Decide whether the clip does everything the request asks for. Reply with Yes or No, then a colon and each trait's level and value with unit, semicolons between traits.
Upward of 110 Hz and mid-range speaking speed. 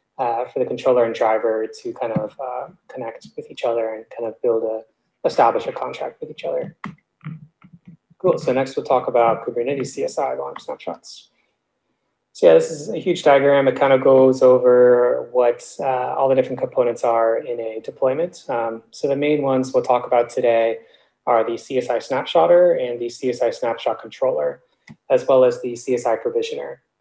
Yes: low, 135 Hz; average, 180 wpm